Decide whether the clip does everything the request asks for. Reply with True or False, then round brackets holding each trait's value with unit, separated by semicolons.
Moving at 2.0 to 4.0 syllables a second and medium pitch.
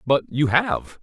True (3.6 syllables/s; 145 Hz)